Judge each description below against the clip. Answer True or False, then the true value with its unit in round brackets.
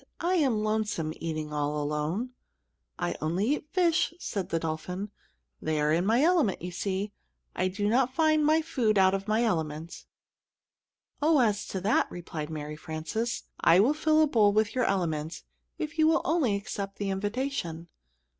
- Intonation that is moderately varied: False (7.9 semitones)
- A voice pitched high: True (205 Hz)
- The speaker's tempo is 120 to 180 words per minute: True (170 wpm)